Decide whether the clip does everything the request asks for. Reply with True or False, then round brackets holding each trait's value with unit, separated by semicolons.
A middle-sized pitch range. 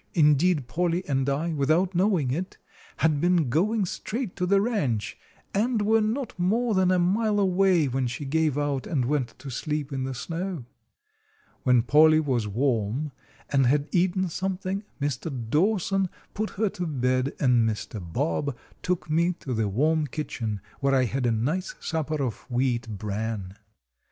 False (6.2 semitones)